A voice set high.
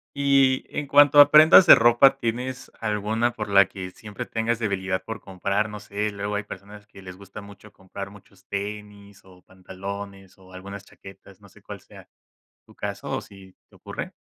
No: low, 100 Hz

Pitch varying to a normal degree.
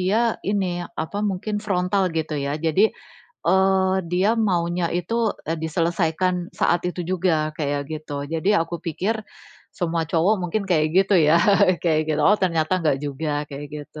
Yes: average, 3.0 semitones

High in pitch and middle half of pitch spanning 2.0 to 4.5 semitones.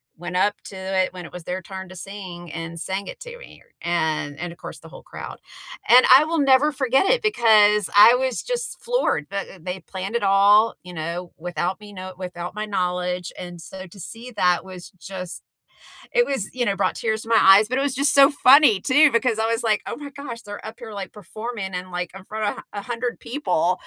No: high, 205 Hz; average, 5.3 semitones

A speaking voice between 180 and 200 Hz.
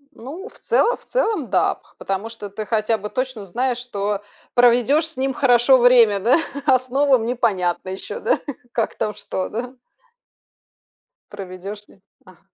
No: high, 235 Hz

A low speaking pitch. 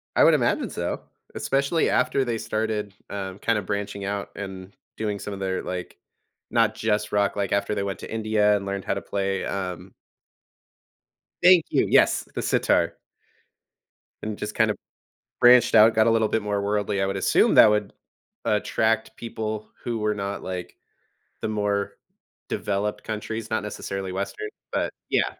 Yes: low, 105 Hz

